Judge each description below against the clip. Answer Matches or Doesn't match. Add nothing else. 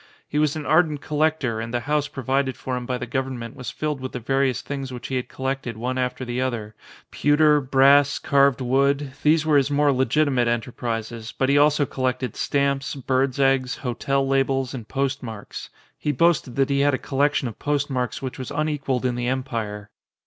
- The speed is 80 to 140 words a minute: Doesn't match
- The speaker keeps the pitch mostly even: Matches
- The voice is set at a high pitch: Doesn't match